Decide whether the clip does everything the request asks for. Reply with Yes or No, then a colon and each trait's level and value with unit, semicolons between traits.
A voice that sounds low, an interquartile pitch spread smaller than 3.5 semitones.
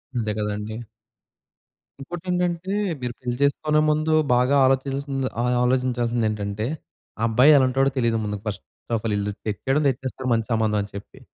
No: low, 125 Hz; average, 4.1 semitones